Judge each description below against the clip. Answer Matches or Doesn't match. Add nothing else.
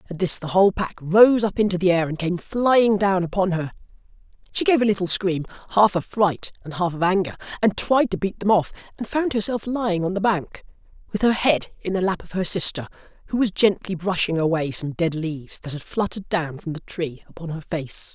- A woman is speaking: Doesn't match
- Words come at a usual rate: Doesn't match